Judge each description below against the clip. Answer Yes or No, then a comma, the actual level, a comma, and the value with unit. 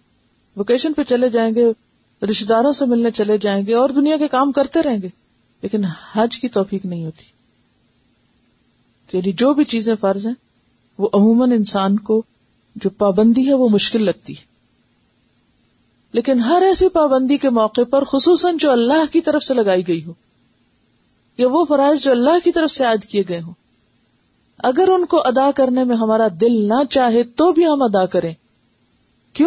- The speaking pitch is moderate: No, high, 235 Hz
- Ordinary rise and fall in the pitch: No, wide, 5.9 semitones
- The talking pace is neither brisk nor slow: Yes, average, 175 wpm